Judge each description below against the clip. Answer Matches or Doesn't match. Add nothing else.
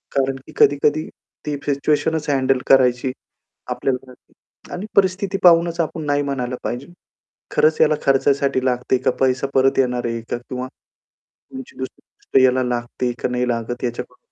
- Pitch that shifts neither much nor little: Matches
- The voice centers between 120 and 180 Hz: Matches